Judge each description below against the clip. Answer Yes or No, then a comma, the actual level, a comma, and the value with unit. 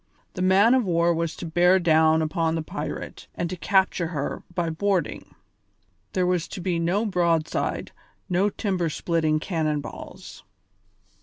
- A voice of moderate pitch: Yes, medium, 170 Hz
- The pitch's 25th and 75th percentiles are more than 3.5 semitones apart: No, narrow, 2.5 semitones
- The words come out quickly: No, average, 150 wpm